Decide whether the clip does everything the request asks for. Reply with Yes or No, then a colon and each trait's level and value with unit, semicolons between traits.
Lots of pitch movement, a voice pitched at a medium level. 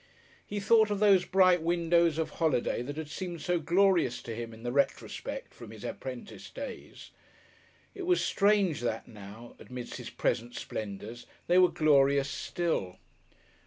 Yes: wide, 7.2 semitones; medium, 160 Hz